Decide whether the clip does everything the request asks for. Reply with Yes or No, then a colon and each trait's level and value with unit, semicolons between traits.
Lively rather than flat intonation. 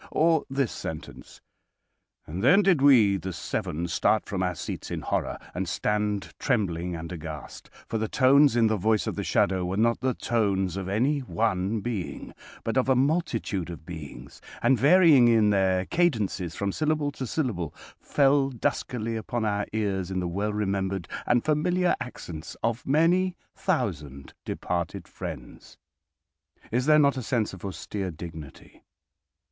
Yes: wide, 6.3 semitones